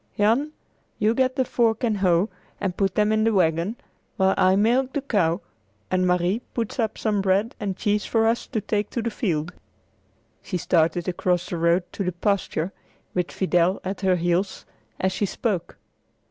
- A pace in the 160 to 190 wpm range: Yes, average, 180 wpm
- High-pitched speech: Yes, high, 195 Hz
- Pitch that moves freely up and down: No, average, 3.7 semitones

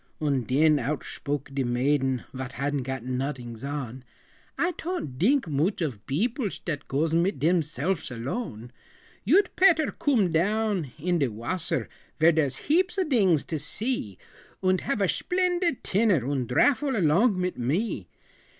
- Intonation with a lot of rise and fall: Yes, wide, 8.3 semitones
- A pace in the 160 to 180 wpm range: No, average, 145 wpm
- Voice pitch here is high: No, medium, 160 Hz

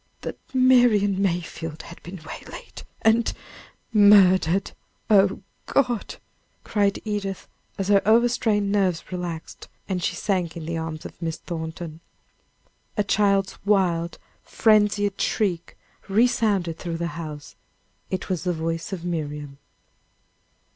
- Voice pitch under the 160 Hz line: No, high, 190 Hz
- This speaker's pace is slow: Yes, slow, 125 wpm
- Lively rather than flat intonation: No, average, 3.7 semitones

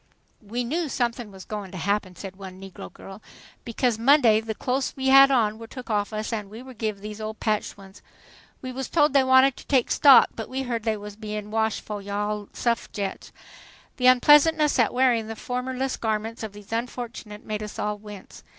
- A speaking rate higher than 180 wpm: Yes, fast, 205 wpm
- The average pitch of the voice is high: Yes, high, 225 Hz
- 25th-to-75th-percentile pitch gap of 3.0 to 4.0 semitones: Yes, average, 3.5 semitones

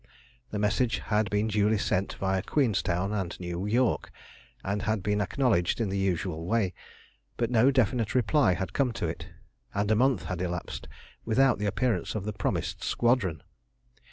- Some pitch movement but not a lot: Yes, average, 3.6 semitones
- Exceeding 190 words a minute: No, average, 165 wpm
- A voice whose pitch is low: Yes, low, 105 Hz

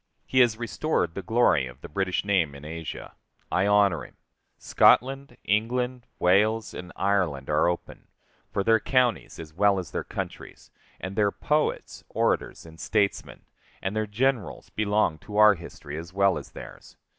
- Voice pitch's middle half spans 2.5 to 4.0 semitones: No, average, 4.7 semitones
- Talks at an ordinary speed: Yes, average, 160 wpm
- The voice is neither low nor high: No, low, 100 Hz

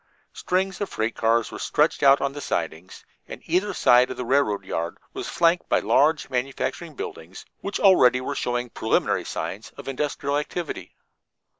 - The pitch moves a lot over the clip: Yes, wide, 5.9 semitones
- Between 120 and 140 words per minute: No, average, 165 wpm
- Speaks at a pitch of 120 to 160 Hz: Yes, low, 135 Hz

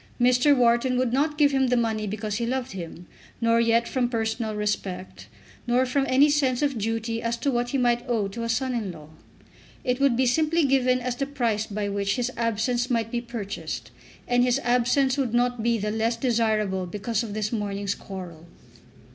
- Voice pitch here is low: No, high, 235 Hz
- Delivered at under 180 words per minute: No, average, 195 wpm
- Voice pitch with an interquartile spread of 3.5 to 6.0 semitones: No, average, 2.9 semitones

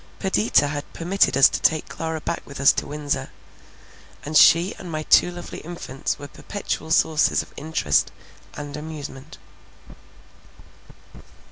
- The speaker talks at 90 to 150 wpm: Yes, slow, 135 wpm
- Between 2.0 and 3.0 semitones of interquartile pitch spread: Yes, narrow, 2.6 semitones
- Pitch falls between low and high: Yes, medium, 155 Hz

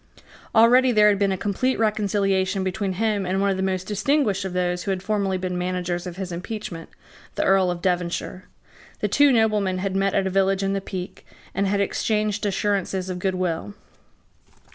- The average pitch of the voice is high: Yes, high, 195 Hz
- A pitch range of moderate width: No, narrow, 2.0 semitones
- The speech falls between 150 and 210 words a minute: Yes, average, 190 wpm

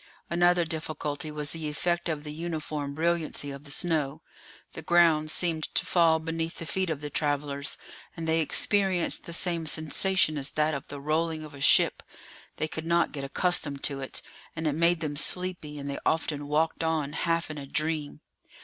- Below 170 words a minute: No, average, 185 wpm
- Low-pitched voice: No, medium, 155 Hz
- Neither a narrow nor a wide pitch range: No, narrow, 2.1 semitones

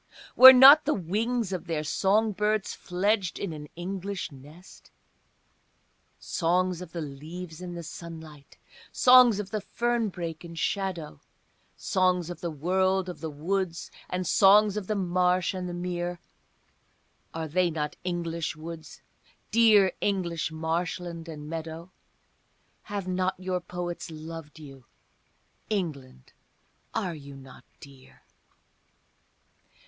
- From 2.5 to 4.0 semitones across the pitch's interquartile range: Yes, average, 3.0 semitones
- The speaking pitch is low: No, medium, 175 Hz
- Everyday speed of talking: No, slow, 125 wpm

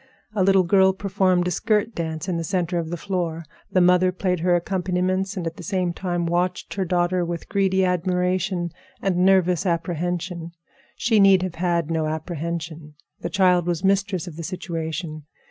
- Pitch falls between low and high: Yes, medium, 180 Hz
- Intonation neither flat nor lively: No, narrow, 1.9 semitones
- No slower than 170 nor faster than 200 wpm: Yes, average, 175 wpm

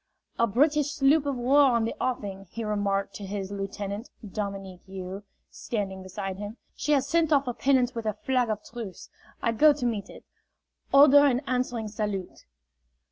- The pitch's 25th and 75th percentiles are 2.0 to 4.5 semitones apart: No, average, 5.2 semitones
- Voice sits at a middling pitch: No, high, 225 Hz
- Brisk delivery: No, average, 175 wpm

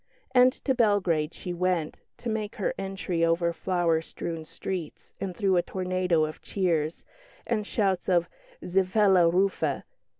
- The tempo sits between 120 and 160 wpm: Yes, average, 140 wpm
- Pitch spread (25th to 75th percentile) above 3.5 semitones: No, narrow, 2.6 semitones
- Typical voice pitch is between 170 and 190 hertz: Yes, medium, 185 Hz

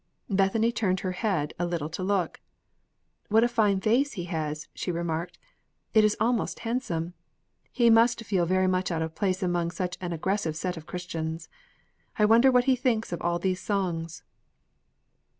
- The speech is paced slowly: No, average, 170 wpm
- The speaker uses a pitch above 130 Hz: Yes, medium, 185 Hz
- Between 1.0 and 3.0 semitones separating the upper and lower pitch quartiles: No, average, 4.4 semitones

